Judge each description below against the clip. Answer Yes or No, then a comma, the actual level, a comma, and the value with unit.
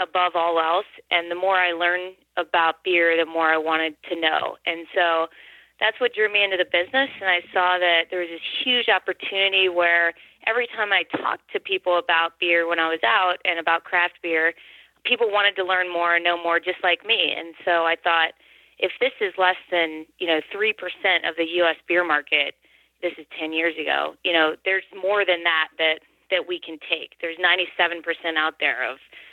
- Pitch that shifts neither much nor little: No, narrow, 2.0 semitones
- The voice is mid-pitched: Yes, medium, 175 Hz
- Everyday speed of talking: No, fast, 215 wpm